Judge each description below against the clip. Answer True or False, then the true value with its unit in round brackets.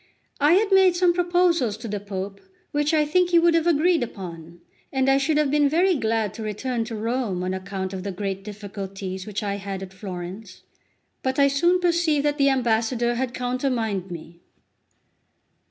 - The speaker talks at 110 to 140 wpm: False (185 wpm)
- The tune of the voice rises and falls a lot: True (7.3 semitones)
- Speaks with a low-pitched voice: False (240 Hz)